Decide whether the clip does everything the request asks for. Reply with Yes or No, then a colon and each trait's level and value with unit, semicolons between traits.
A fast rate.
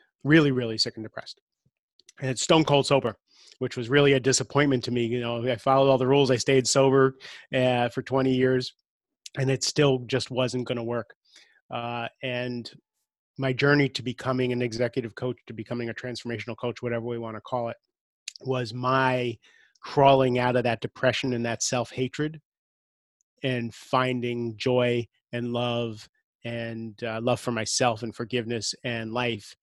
No: average, 170 wpm